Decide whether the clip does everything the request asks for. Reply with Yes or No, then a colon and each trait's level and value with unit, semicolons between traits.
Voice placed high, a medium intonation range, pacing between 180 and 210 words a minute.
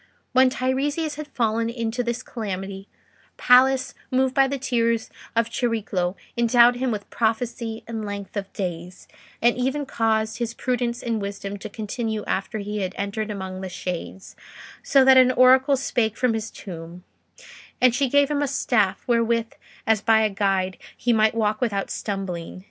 No: high, 225 Hz; average, 3.8 semitones; average, 165 wpm